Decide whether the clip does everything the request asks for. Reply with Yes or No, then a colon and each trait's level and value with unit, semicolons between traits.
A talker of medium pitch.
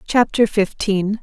No: high, 210 Hz